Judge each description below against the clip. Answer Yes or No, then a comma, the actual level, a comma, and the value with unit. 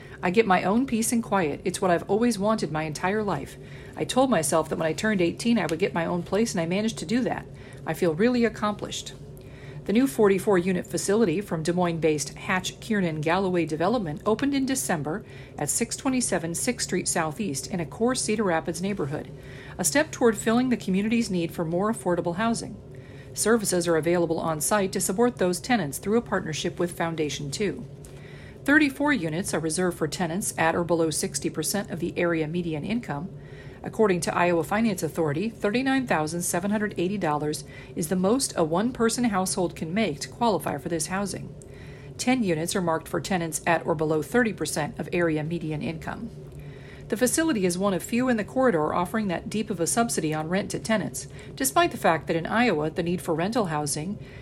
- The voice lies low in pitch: No, medium, 180 Hz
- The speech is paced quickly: No, average, 190 wpm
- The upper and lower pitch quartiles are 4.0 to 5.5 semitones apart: Yes, average, 5.2 semitones